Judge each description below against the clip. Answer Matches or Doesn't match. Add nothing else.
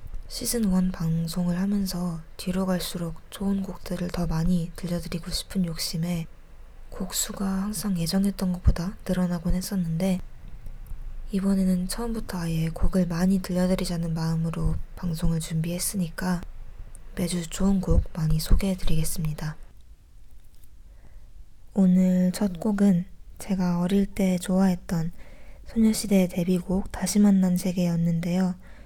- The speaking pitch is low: Doesn't match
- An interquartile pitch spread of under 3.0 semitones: Matches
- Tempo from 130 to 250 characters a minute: Doesn't match